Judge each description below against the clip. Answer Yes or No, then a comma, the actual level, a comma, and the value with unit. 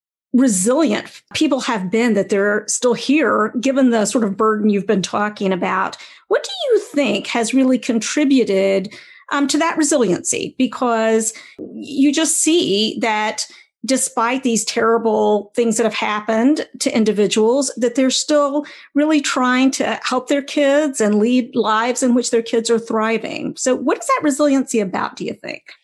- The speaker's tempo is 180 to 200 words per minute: No, average, 160 wpm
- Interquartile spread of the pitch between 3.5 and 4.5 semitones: Yes, average, 4.1 semitones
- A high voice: Yes, high, 245 Hz